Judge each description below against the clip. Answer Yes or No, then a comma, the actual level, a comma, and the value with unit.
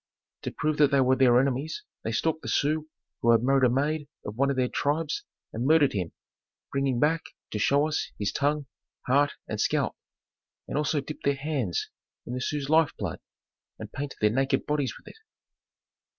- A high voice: No, medium, 140 Hz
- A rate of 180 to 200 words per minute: Yes, average, 190 wpm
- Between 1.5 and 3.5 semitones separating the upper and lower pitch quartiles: Yes, average, 2.8 semitones